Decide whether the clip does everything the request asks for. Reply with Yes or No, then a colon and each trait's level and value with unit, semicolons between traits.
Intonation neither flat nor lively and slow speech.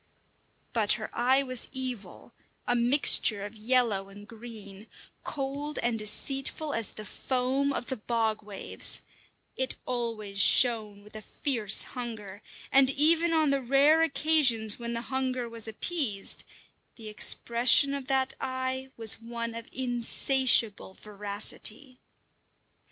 Yes: average, 3.7 semitones; slow, 130 wpm